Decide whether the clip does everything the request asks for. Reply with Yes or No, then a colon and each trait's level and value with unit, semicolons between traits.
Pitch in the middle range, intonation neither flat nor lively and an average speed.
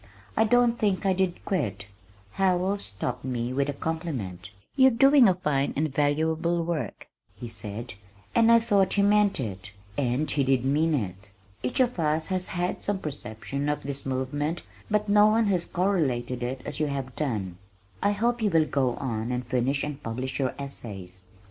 No: medium, 145 Hz; wide, 7.2 semitones; average, 180 wpm